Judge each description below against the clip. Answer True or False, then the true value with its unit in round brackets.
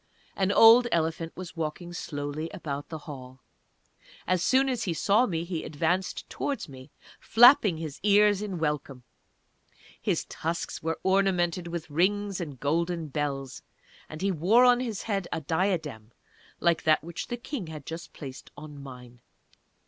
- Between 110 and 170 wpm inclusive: True (155 wpm)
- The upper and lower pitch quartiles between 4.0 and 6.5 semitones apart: True (4.7 semitones)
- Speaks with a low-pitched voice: False (170 Hz)